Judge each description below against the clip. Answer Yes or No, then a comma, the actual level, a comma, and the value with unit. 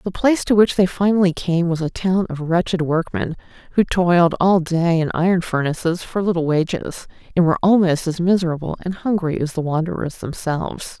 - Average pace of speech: Yes, average, 185 wpm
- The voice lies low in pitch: No, medium, 175 Hz